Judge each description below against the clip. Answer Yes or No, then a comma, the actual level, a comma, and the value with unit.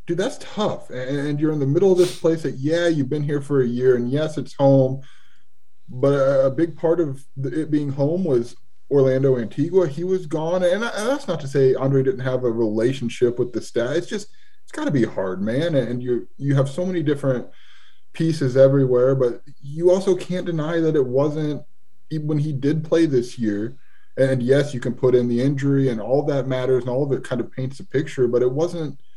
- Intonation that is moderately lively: Yes, average, 3.5 semitones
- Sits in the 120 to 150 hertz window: Yes, medium, 140 Hz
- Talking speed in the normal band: No, fast, 220 wpm